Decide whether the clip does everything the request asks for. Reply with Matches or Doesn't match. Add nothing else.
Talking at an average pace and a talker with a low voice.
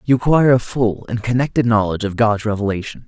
Matches